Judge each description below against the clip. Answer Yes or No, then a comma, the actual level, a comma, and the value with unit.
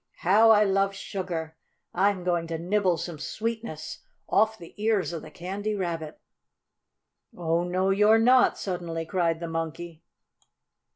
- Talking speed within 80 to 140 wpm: Yes, slow, 135 wpm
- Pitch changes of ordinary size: Yes, average, 3.6 semitones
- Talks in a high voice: No, medium, 180 Hz